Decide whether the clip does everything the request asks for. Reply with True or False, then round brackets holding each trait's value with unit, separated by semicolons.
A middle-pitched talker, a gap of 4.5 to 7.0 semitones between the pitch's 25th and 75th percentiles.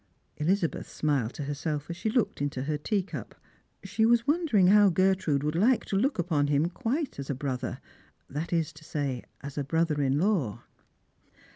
True (160 Hz; 5.5 semitones)